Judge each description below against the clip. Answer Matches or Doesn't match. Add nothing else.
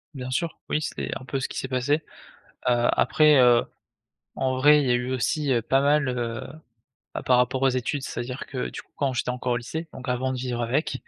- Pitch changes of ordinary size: Doesn't match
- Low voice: Matches